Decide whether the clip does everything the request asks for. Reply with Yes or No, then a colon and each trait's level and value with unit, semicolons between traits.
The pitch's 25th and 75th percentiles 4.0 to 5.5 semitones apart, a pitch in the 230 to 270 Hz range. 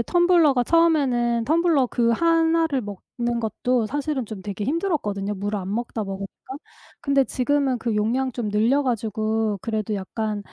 Yes: average, 5.1 semitones; high, 240 Hz